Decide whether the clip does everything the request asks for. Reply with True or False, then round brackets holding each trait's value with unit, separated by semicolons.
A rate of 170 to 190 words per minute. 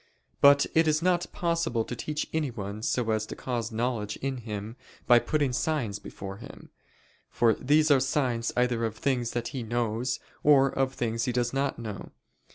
True (175 wpm)